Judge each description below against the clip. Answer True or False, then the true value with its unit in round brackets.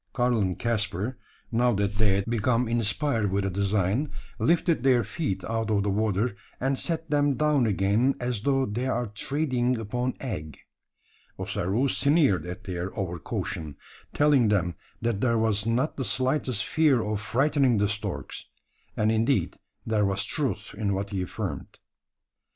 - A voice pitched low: True (115 Hz)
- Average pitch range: True (4.4 semitones)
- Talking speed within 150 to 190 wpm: True (155 wpm)